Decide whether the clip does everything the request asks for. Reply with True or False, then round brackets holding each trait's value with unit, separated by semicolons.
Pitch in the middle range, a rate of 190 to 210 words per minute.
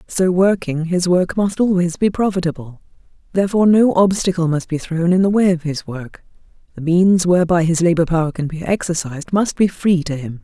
True (175 Hz; 195 wpm)